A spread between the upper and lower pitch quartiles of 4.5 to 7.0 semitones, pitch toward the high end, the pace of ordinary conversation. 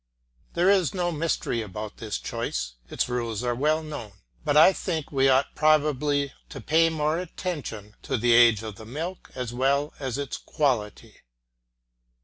No: average, 5.0 semitones; medium, 140 Hz; average, 160 wpm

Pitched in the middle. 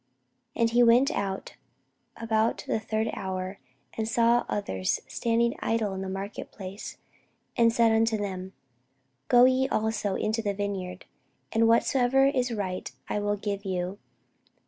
No: high, 220 Hz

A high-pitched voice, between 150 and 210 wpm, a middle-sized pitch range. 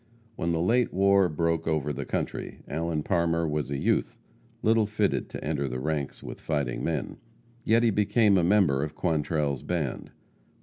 No: very low, 85 Hz; average, 170 wpm; average, 4.9 semitones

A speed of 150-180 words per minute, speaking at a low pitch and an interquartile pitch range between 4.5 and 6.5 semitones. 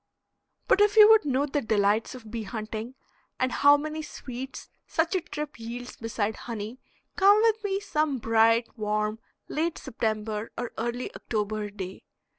No: average, 155 wpm; high, 240 Hz; wide, 5.6 semitones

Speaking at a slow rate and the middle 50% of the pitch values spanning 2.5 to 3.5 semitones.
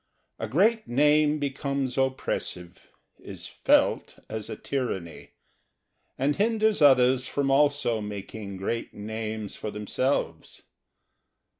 No: slow, 105 wpm; average, 5.0 semitones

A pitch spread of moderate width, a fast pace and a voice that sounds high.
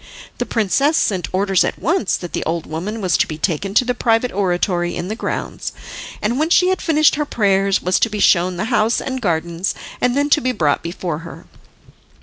No: wide, 6.0 semitones; fast, 210 wpm; high, 200 Hz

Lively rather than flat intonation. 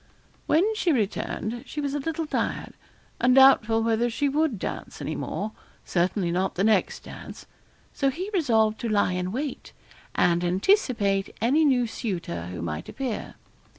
Yes: wide, 6.5 semitones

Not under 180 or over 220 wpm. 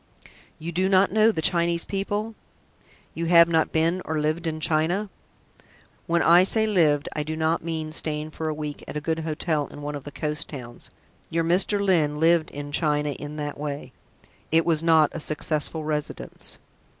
Yes: average, 185 wpm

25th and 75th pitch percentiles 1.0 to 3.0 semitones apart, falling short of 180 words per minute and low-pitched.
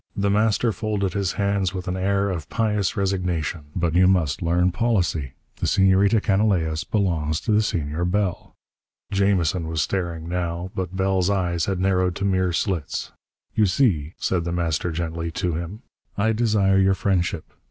Yes: average, 2.7 semitones; average, 165 wpm; very low, 95 Hz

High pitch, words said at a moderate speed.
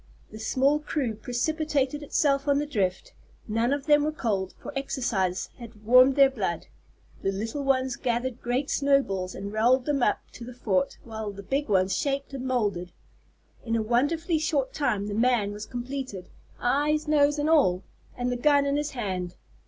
Yes: very high, 250 Hz; average, 175 wpm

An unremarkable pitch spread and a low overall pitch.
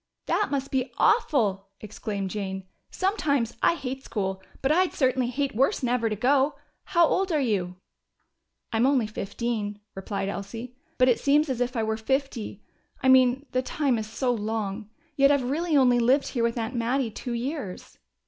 No: average, 4.1 semitones; high, 245 Hz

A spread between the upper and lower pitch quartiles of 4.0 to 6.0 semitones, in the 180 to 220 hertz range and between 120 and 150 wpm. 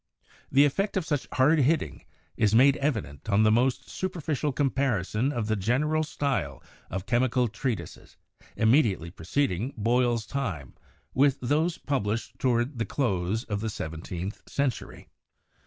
No: average, 5.2 semitones; low, 120 Hz; average, 140 wpm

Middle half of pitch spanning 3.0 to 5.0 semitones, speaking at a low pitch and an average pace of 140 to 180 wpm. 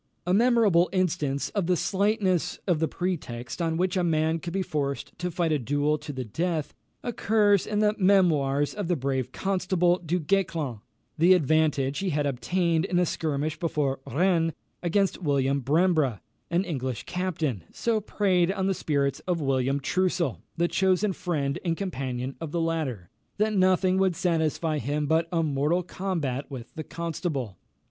No: average, 4.5 semitones; medium, 165 Hz; average, 165 wpm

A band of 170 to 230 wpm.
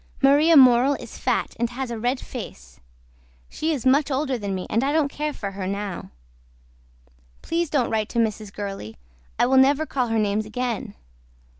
Yes: average, 180 wpm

